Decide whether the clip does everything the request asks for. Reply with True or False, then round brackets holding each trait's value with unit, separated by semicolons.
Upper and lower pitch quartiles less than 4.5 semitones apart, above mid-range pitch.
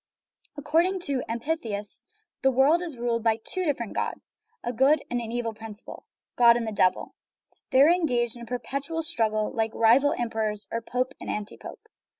True (4.1 semitones; 240 Hz)